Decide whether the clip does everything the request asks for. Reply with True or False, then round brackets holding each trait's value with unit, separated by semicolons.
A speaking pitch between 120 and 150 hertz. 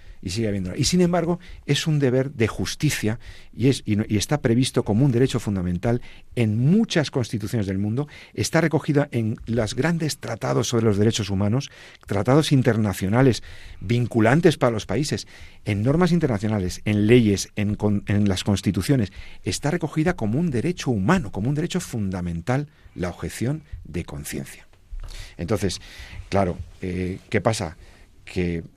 False (110 Hz)